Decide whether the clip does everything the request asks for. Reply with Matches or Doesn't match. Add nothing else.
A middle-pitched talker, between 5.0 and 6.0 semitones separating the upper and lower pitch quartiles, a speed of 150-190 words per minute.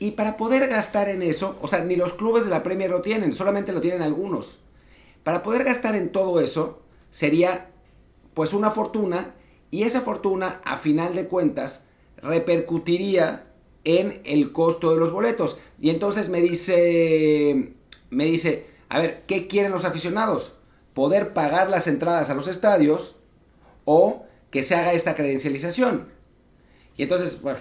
Doesn't match